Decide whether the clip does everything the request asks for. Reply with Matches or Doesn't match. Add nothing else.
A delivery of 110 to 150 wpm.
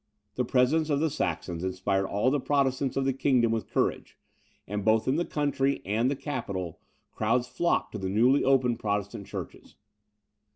Doesn't match